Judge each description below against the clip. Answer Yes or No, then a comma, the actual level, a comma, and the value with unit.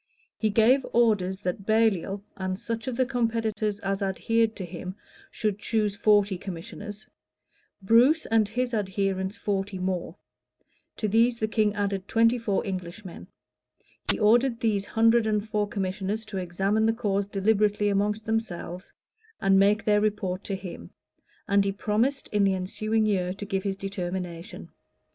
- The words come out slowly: No, average, 150 wpm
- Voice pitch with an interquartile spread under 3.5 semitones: Yes, narrow, 2.4 semitones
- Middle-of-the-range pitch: No, high, 205 Hz